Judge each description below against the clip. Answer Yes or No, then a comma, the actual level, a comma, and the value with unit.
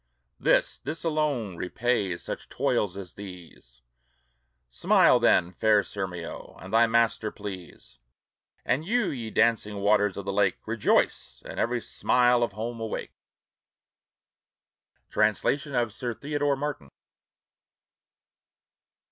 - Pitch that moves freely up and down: No, average, 4.0 semitones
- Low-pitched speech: Yes, low, 110 Hz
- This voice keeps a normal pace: No, slow, 115 wpm